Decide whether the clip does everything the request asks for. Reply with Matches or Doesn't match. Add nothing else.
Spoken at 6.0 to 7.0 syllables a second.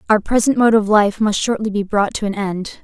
Doesn't match